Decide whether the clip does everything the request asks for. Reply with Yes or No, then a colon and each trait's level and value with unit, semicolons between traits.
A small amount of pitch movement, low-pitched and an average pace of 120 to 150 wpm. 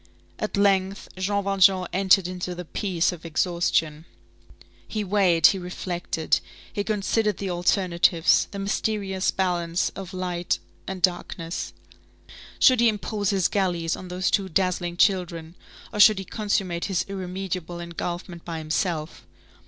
No: narrow, 2.3 semitones; medium, 185 Hz; slow, 135 wpm